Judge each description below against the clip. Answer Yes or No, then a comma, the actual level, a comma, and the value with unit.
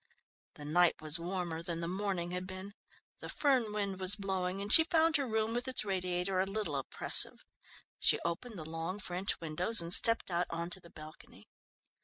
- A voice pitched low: No, medium, 185 Hz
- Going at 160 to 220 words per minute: Yes, average, 190 wpm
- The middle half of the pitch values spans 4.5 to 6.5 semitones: No, average, 3.5 semitones